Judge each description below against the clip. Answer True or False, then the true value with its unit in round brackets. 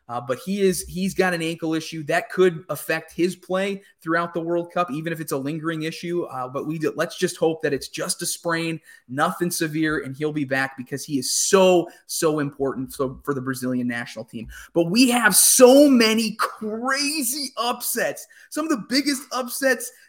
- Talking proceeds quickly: False (195 wpm)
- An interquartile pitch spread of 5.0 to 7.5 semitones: True (5.5 semitones)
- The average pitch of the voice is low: False (170 Hz)